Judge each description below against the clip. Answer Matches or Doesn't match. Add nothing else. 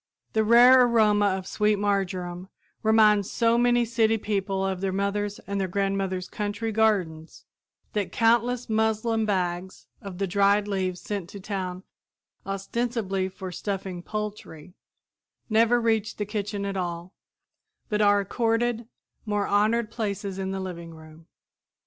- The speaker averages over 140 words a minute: Doesn't match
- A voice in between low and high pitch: Doesn't match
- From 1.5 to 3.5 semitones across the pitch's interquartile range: Matches